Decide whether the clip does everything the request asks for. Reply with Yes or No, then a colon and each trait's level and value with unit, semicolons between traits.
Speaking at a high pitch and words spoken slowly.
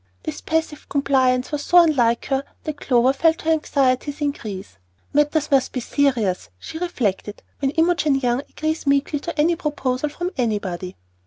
No: very high, 280 Hz; average, 155 wpm